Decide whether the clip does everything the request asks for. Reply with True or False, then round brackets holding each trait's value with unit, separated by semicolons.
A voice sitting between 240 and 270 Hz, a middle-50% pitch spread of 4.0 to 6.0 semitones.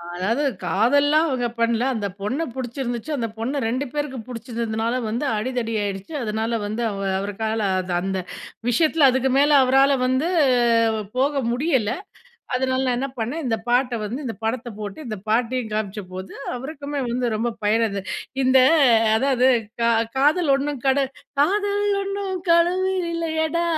True (255 Hz; 4.4 semitones)